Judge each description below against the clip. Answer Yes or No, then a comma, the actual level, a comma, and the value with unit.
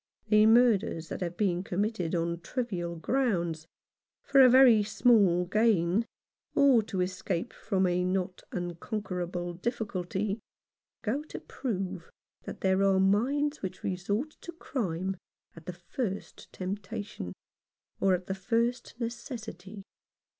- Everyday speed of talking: No, slow, 125 wpm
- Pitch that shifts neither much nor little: Yes, average, 4.3 semitones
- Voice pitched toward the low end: No, high, 195 Hz